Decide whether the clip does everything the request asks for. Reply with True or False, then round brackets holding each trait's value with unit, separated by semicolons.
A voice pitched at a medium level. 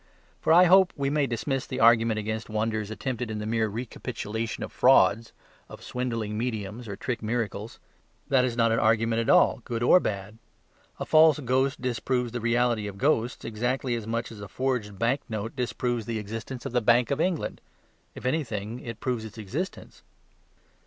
False (115 Hz)